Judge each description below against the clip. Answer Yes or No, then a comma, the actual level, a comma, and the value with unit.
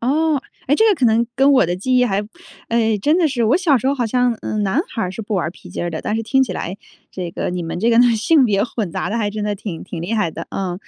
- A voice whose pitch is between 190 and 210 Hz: No, high, 225 Hz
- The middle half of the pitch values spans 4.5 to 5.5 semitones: Yes, average, 5.1 semitones